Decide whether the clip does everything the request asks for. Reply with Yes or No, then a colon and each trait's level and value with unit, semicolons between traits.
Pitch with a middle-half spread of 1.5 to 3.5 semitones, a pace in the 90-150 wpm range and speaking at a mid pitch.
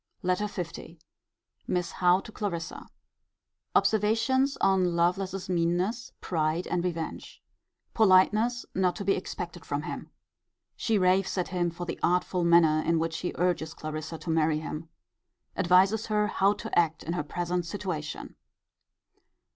Yes: average, 2.7 semitones; average, 140 wpm; medium, 180 Hz